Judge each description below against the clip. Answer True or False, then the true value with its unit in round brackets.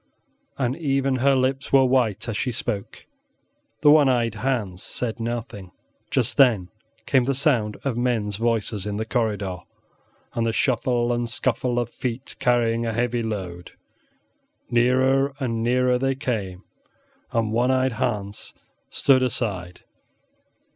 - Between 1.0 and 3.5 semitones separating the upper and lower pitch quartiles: True (3.0 semitones)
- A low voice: True (120 Hz)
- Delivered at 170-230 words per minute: False (140 wpm)